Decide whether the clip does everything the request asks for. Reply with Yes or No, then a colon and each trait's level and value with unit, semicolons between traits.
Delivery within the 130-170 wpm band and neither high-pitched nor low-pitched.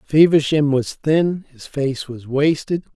Yes: average, 140 wpm; medium, 145 Hz